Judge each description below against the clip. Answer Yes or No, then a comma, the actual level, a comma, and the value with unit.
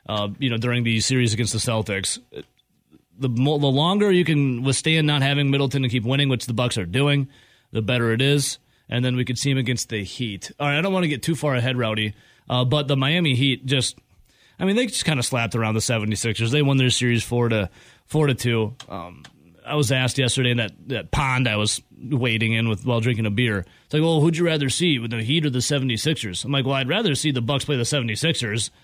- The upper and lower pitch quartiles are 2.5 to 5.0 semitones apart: Yes, average, 3.8 semitones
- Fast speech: Yes, fast, 245 wpm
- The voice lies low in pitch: Yes, low, 125 Hz